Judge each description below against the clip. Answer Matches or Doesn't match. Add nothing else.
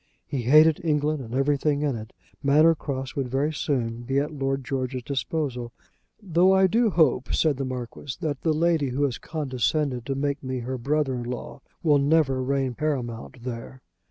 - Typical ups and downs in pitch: Matches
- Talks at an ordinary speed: Matches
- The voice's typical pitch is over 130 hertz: Matches